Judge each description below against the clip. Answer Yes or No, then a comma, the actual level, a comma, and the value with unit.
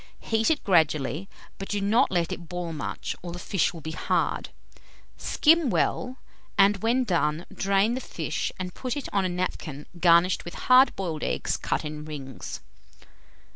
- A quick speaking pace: No, average, 170 wpm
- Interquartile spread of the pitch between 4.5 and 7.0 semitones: Yes, average, 5.0 semitones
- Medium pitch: Yes, medium, 180 Hz